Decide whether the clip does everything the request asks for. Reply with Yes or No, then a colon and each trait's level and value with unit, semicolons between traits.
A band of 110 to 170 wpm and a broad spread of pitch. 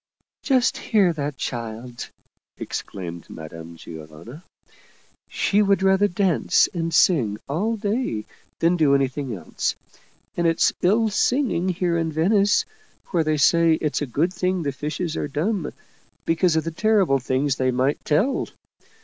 Yes: average, 155 wpm; wide, 6.1 semitones